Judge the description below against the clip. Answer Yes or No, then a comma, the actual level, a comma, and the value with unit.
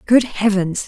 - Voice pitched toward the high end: Yes, high, 210 Hz